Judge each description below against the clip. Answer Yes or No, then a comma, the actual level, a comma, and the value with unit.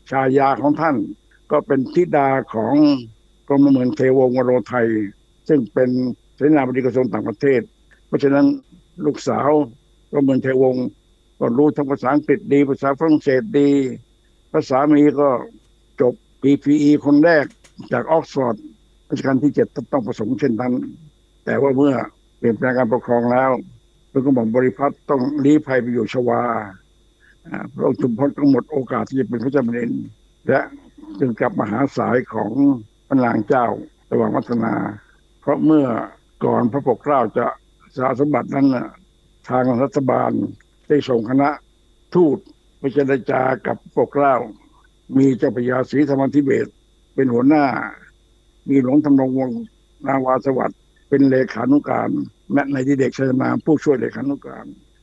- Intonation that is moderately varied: No, narrow, 2.3 semitones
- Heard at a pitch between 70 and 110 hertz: No, low, 135 Hz